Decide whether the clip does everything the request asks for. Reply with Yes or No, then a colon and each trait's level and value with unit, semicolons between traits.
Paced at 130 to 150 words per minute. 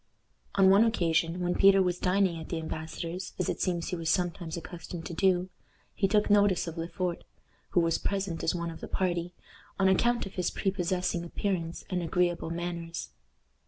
No: average, 185 wpm